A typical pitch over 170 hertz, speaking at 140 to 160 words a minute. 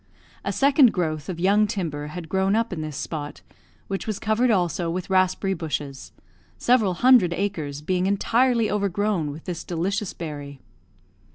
Yes: medium, 185 Hz; average, 155 wpm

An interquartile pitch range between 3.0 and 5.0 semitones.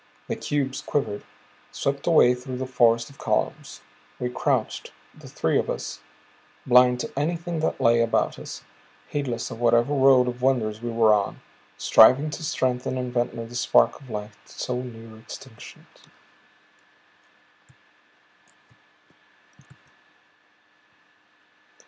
No: narrow, 2.6 semitones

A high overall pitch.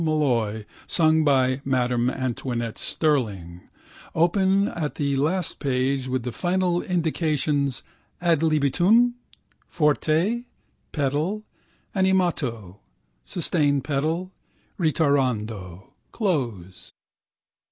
No: medium, 145 Hz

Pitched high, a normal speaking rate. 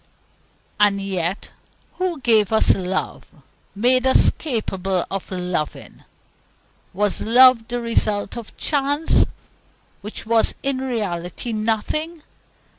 No: high, 220 Hz; slow, 105 wpm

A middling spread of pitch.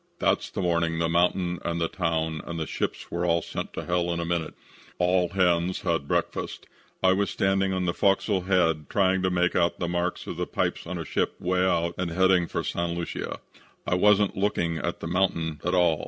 No: narrow, 1.7 semitones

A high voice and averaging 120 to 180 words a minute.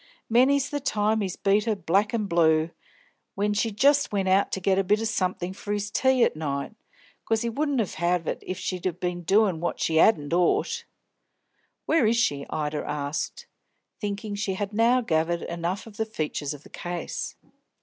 No: high, 195 Hz; average, 190 wpm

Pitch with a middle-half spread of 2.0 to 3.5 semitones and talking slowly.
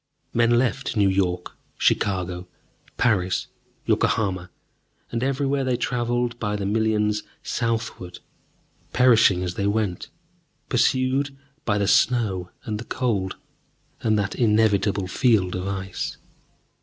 No: average, 4.0 semitones; slow, 115 wpm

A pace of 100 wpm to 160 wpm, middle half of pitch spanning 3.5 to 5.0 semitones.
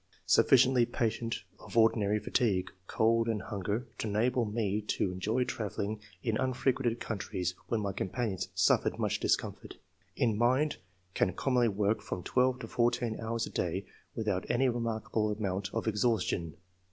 No: average, 150 wpm; average, 3.0 semitones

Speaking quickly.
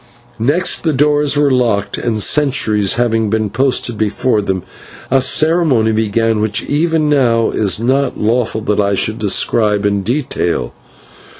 No: average, 145 wpm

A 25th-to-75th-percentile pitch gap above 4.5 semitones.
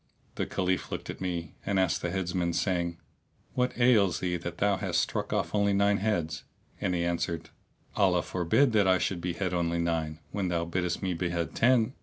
No: average, 2.8 semitones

